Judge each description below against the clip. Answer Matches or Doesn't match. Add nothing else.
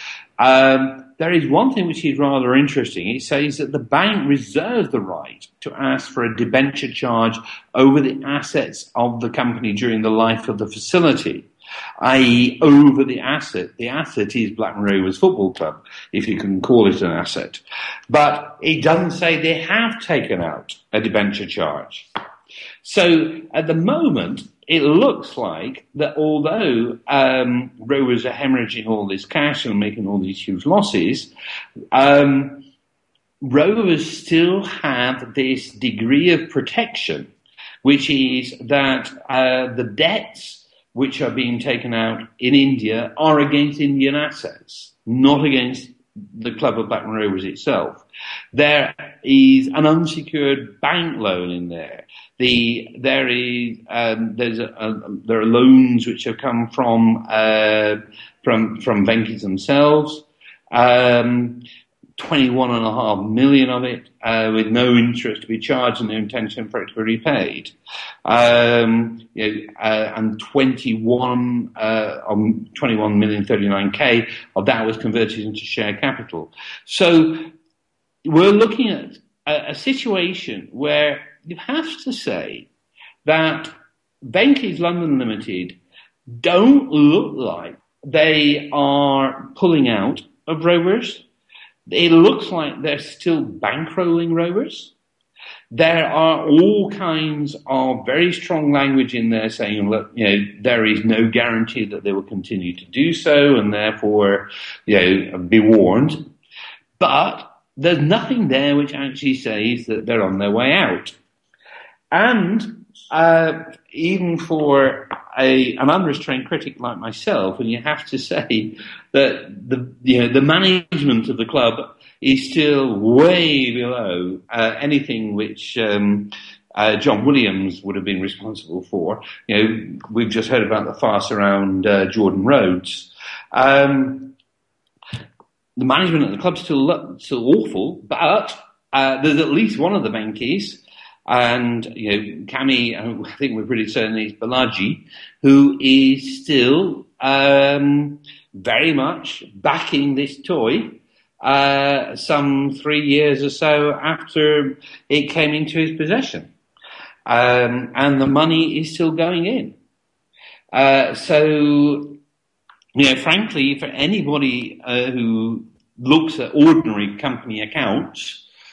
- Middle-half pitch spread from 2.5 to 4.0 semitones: Doesn't match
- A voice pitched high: Doesn't match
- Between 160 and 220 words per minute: Doesn't match